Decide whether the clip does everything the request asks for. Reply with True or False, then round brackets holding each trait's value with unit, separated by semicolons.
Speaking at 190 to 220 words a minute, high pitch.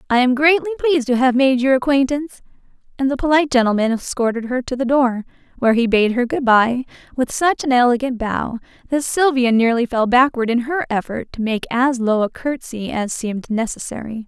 True (195 wpm; 250 Hz)